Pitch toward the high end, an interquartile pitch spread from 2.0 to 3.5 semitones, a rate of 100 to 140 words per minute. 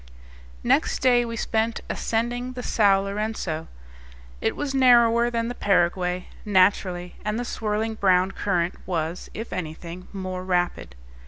No: high, 200 Hz; average, 4.2 semitones; slow, 135 wpm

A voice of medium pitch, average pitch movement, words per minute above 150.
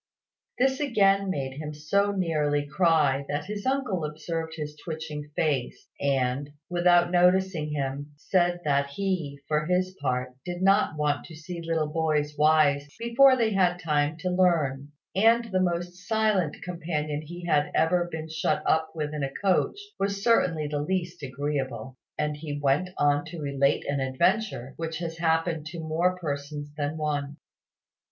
Yes: medium, 160 Hz; average, 3.6 semitones; average, 160 wpm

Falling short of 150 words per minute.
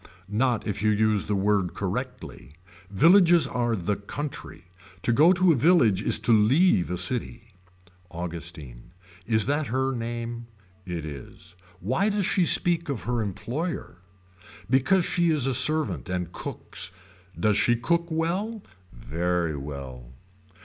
Yes: average, 140 wpm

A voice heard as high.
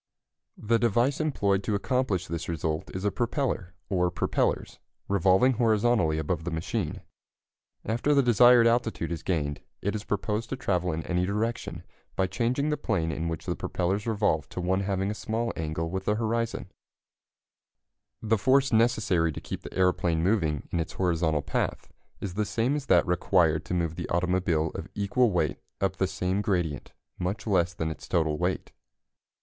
No: very low, 95 Hz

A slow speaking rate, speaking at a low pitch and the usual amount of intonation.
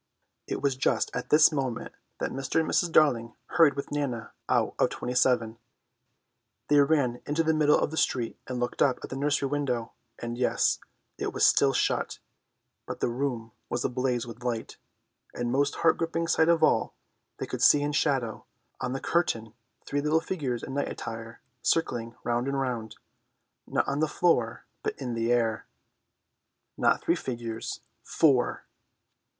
No: average, 165 wpm; low, 130 Hz; average, 3.7 semitones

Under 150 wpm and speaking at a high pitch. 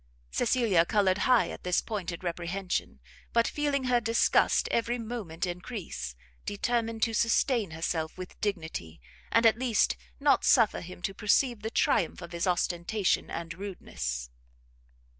Yes: average, 140 wpm; high, 200 Hz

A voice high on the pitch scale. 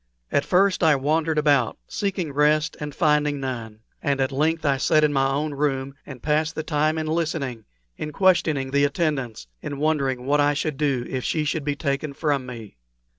No: medium, 145 Hz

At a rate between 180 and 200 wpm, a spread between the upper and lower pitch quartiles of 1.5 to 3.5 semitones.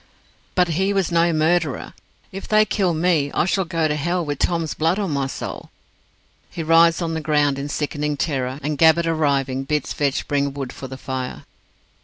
Yes: average, 190 wpm; average, 3.2 semitones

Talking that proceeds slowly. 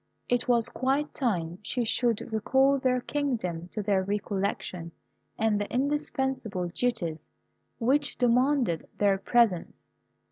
Yes: slow, 115 wpm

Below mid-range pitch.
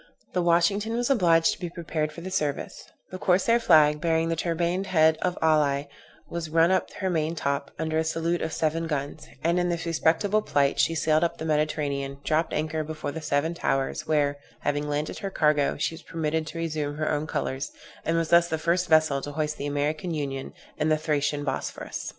No: medium, 160 Hz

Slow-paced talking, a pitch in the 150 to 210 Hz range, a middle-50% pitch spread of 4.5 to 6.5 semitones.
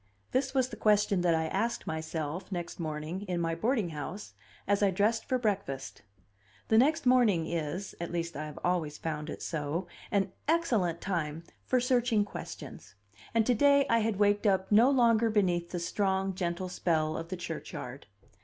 No: average, 175 wpm; medium, 185 Hz; average, 5.1 semitones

